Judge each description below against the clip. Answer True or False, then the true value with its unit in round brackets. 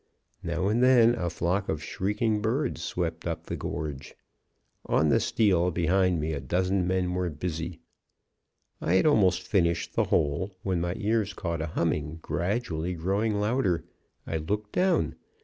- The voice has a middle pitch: False (90 Hz)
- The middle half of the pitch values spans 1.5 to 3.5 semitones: False (3.9 semitones)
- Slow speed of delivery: False (155 wpm)